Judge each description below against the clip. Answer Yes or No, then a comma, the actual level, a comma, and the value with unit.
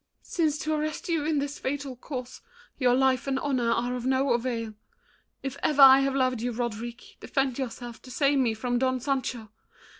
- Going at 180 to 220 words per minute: Yes, average, 185 wpm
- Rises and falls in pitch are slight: Yes, narrow, 2.3 semitones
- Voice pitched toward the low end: No, very high, 260 Hz